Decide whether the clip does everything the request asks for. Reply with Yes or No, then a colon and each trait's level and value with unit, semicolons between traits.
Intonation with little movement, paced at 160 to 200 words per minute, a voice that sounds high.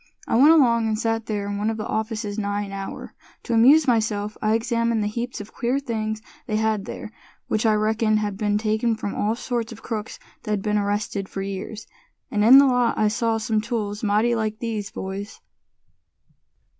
Yes: narrow, 1.8 semitones; average, 195 wpm; high, 215 Hz